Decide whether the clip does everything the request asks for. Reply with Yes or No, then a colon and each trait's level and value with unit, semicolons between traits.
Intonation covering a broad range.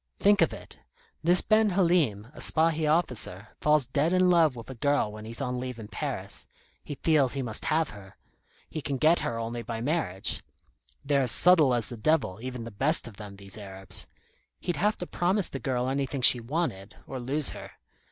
Yes: wide, 5.9 semitones